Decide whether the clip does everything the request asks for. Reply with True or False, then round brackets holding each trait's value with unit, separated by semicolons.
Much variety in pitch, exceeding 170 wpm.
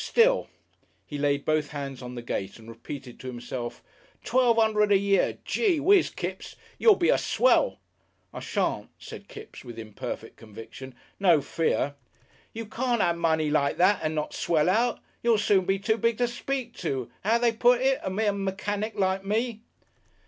True (8.5 semitones; 180 wpm)